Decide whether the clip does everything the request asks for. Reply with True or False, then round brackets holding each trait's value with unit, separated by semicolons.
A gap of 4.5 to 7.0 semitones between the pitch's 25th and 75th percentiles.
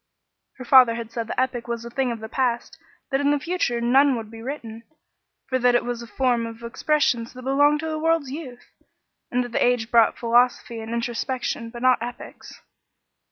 False (2.4 semitones)